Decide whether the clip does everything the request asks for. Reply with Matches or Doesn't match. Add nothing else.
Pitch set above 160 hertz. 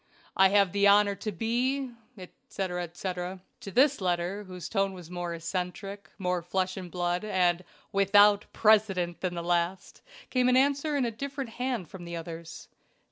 Matches